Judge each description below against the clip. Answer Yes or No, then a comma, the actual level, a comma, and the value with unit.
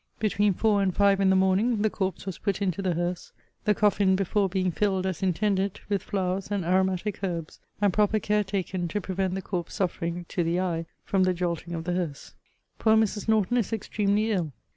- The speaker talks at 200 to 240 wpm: Yes, fast, 205 wpm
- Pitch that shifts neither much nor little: No, narrow, 2.3 semitones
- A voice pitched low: No, high, 190 Hz